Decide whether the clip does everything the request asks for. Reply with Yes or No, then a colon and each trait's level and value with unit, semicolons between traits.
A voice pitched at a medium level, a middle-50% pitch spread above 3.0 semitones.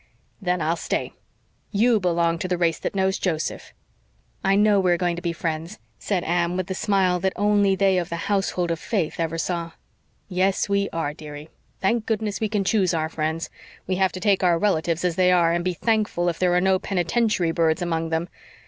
No: medium, 180 Hz; average, 2.7 semitones